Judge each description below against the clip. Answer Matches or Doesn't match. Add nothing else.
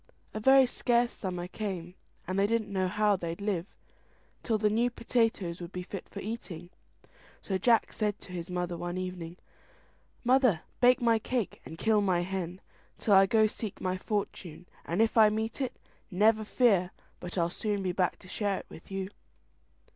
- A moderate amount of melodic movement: Matches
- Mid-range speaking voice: Doesn't match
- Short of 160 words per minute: Doesn't match